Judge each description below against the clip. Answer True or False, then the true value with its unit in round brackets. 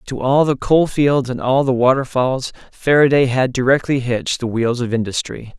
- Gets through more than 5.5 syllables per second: False (4.9 syllables/s)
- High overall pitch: False (130 Hz)